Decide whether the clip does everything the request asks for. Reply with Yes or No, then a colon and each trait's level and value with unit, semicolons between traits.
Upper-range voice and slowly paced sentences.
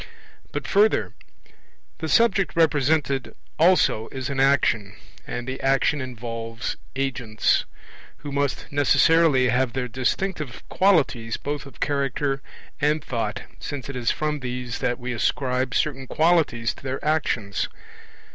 No: low, 135 Hz; slow, 130 wpm